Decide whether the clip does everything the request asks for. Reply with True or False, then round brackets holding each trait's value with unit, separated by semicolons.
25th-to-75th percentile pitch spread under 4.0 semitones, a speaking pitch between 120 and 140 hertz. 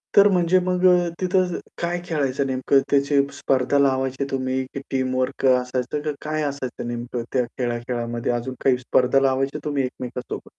True (2.6 semitones; 135 Hz)